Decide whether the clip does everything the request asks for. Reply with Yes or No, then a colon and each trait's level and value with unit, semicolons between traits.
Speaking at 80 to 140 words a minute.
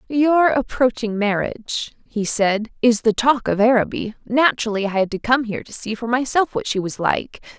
No: average, 190 wpm